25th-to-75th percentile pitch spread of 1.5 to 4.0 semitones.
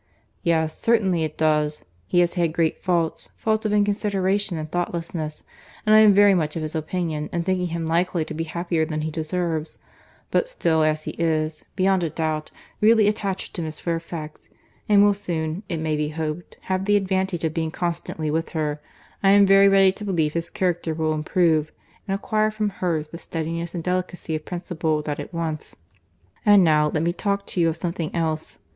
Yes: average, 3.3 semitones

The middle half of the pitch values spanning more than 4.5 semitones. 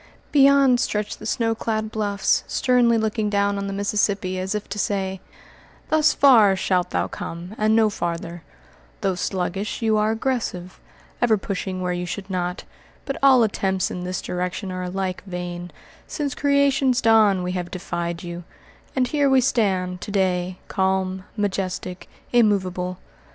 No: average, 3.6 semitones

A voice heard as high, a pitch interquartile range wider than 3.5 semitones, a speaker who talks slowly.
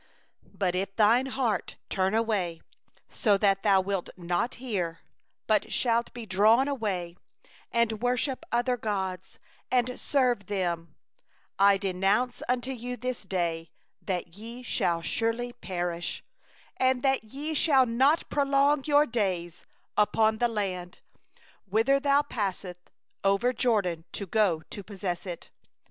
Yes: high, 210 Hz; average, 4.9 semitones; slow, 125 wpm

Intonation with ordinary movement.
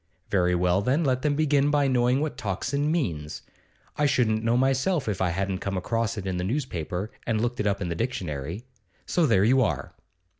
No: wide, 6.4 semitones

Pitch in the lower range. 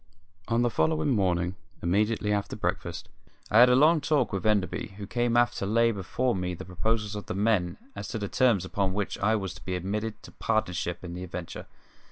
Yes: low, 105 Hz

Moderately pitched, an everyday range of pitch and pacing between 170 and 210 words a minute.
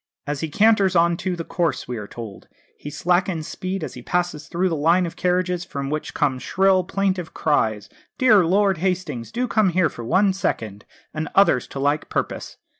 Yes: medium, 175 Hz; average, 4.2 semitones; average, 190 wpm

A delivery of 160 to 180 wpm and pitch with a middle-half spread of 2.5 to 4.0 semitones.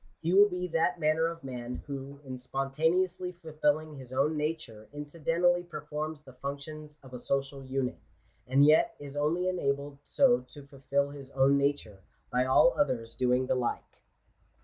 Yes: average, 170 wpm; average, 3.1 semitones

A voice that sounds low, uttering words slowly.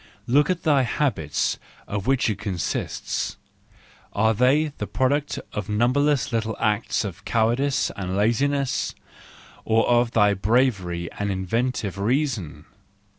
Yes: low, 115 Hz; slow, 125 wpm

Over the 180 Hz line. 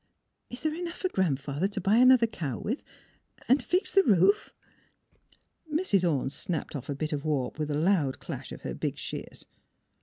Yes: high, 190 Hz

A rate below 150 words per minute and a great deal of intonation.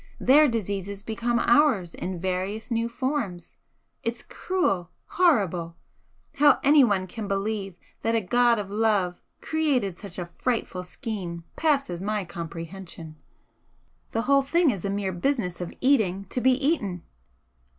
Yes: slow, 135 wpm; wide, 5.8 semitones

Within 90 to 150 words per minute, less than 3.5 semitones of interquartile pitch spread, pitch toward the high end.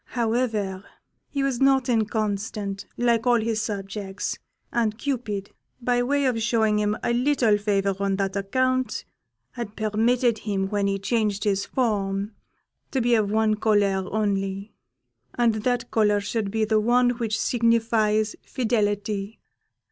Yes: average, 140 wpm; average, 2.8 semitones; high, 220 Hz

